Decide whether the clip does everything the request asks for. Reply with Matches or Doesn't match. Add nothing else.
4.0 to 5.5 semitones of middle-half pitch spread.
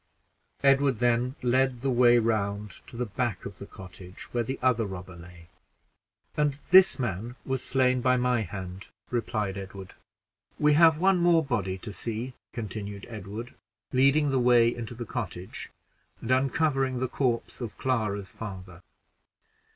Matches